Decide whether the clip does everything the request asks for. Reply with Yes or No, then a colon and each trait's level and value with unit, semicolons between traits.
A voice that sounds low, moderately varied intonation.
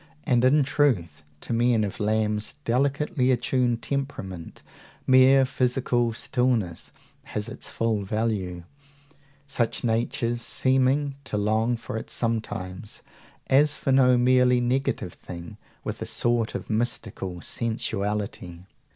Yes: low, 120 Hz; average, 3.5 semitones